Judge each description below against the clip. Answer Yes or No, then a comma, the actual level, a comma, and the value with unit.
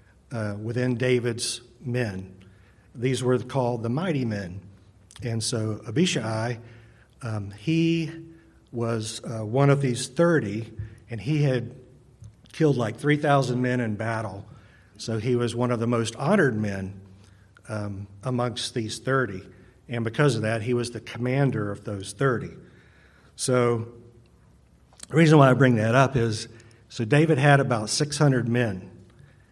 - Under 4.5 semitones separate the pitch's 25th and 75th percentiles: Yes, average, 3.1 semitones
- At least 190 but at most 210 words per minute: No, average, 140 wpm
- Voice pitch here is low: Yes, low, 120 Hz